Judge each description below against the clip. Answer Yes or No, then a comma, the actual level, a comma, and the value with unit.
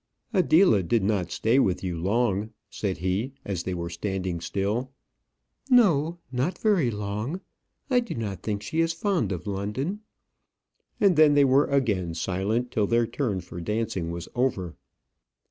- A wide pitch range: Yes, wide, 6.9 semitones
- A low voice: Yes, low, 110 Hz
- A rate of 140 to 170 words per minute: Yes, average, 155 wpm